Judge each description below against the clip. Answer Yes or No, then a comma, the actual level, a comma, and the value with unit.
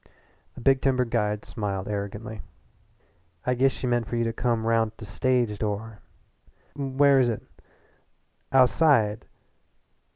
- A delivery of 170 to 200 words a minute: No, average, 140 wpm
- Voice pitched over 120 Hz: No, low, 115 Hz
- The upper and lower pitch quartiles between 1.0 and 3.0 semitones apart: No, average, 3.4 semitones